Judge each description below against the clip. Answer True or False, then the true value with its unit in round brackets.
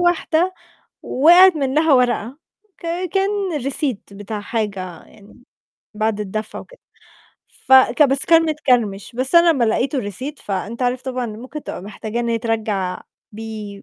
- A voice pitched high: True (245 Hz)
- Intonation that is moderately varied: False (6.0 semitones)